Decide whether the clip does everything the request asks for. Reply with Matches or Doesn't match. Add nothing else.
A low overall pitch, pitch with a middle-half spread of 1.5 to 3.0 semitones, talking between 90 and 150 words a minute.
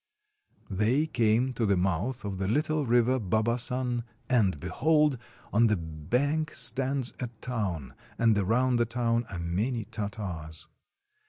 Doesn't match